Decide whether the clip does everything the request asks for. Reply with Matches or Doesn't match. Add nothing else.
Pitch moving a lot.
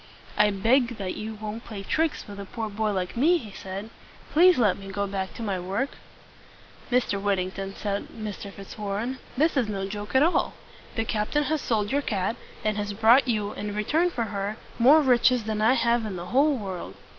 Doesn't match